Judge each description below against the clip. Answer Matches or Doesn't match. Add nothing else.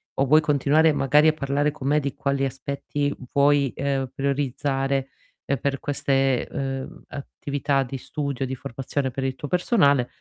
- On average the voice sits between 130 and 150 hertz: Matches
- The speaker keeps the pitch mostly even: Matches